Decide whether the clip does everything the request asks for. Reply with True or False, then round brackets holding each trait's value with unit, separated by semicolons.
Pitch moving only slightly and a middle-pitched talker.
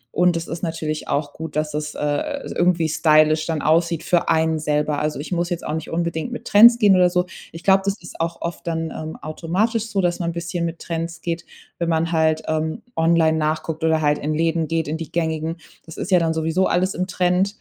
True (1.8 semitones; 165 Hz)